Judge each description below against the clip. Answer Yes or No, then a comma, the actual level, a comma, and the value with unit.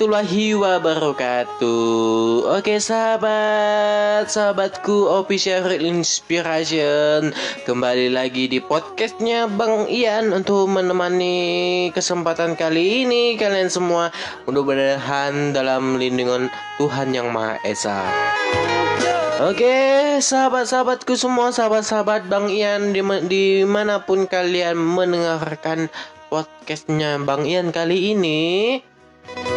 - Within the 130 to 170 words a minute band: No, slow, 85 wpm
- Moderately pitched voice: Yes, medium, 180 Hz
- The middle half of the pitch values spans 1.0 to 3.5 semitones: No, wide, 5.5 semitones